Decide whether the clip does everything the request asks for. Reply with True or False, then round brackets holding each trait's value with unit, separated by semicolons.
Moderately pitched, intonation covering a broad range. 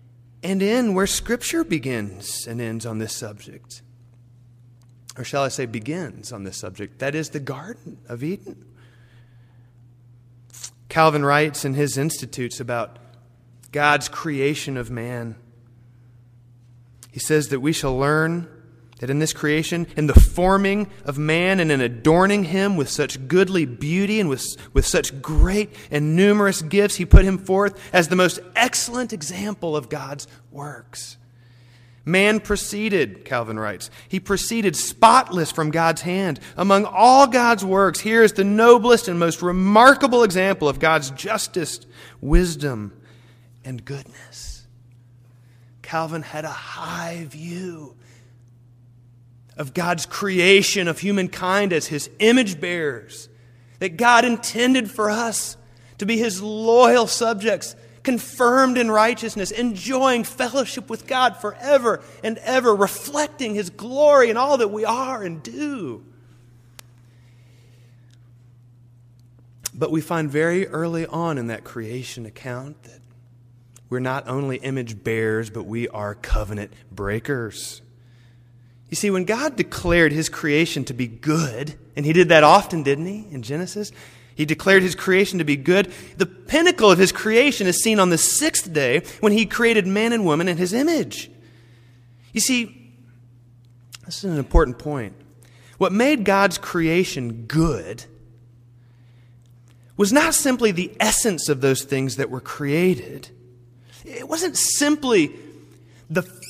True (150 Hz; 8.3 semitones)